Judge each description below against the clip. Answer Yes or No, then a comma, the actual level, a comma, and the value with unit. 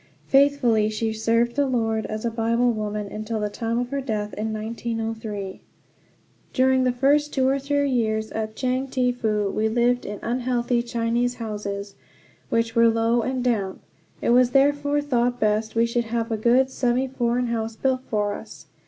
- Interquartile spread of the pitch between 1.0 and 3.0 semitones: Yes, narrow, 2.5 semitones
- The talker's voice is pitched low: No, high, 235 Hz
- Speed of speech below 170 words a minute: No, average, 180 wpm